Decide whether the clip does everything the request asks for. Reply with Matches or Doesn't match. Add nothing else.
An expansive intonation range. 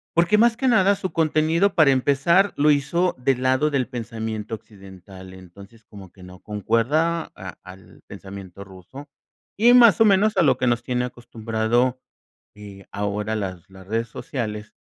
Matches